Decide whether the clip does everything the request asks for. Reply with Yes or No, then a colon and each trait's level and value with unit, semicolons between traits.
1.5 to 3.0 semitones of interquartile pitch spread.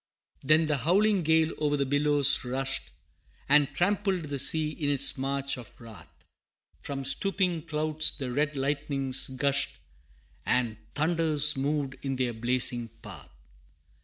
Yes: average, 2.7 semitones